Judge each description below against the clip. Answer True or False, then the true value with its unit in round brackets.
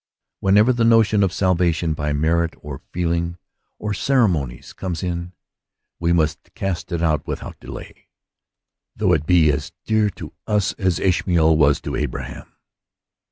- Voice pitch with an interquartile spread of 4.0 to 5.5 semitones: False (3.6 semitones)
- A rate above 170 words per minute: False (145 wpm)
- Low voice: True (85 Hz)